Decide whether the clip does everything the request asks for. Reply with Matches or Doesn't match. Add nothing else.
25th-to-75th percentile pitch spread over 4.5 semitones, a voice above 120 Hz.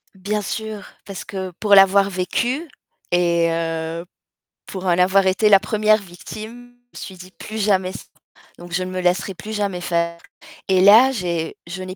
Doesn't match